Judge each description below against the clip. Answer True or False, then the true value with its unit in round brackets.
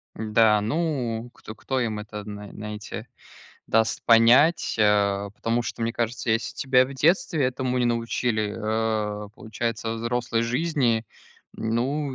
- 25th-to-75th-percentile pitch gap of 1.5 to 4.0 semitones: True (2.6 semitones)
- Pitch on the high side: False (115 Hz)